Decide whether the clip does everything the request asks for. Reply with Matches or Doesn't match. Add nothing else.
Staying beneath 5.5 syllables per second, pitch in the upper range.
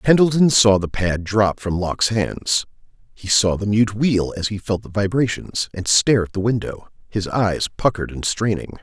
Doesn't match